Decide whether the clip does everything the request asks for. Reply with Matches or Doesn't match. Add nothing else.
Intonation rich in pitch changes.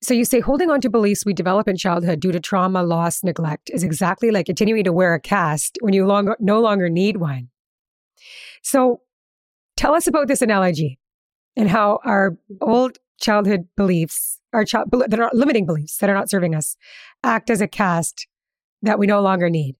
Doesn't match